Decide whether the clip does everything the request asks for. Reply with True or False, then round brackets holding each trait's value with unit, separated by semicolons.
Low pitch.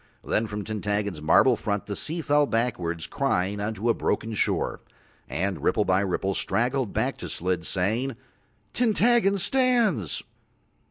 True (110 Hz)